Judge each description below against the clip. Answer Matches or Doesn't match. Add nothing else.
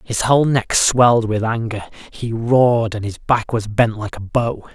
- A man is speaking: Matches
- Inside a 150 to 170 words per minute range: Doesn't match